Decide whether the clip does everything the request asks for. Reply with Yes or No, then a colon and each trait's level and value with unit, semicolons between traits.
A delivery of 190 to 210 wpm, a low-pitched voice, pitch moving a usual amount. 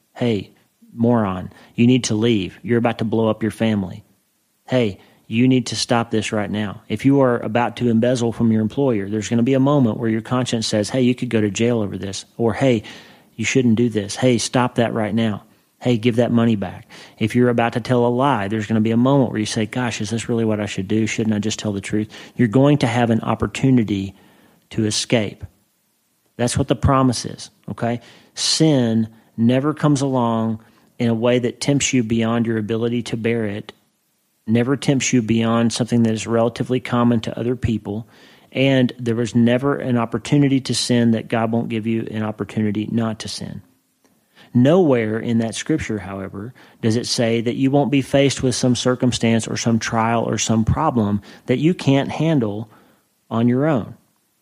No: average, 200 wpm; low, 115 Hz; narrow, 2.2 semitones